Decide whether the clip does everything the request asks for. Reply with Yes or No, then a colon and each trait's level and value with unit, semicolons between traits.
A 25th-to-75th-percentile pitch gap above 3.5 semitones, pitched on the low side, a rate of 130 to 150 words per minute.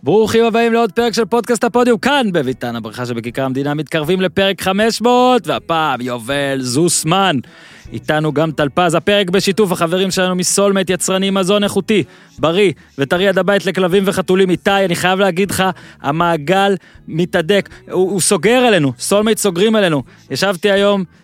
No: average, 4.1 semitones; high, 190 Hz; average, 145 wpm